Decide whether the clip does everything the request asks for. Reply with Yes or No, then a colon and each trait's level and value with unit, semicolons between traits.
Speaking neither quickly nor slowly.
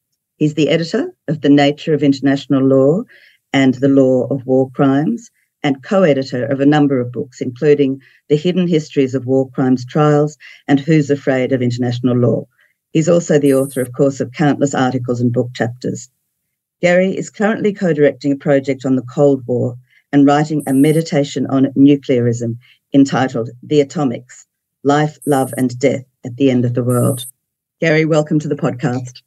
Yes: average, 170 wpm